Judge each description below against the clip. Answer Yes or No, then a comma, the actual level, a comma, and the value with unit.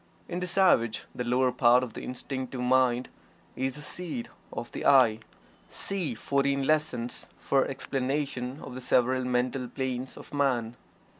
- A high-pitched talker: No, low, 130 Hz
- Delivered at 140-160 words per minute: Yes, average, 150 wpm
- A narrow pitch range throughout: Yes, narrow, 2.0 semitones